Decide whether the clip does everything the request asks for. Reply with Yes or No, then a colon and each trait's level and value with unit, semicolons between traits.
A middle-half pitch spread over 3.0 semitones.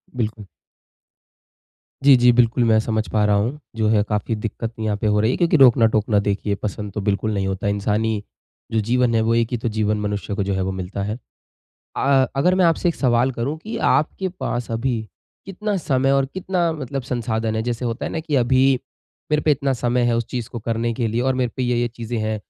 Yes: average, 3.5 semitones